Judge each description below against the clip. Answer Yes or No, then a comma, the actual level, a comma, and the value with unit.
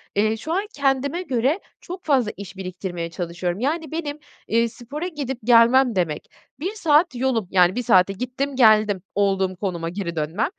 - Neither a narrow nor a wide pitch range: No, wide, 6.9 semitones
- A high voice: Yes, high, 230 Hz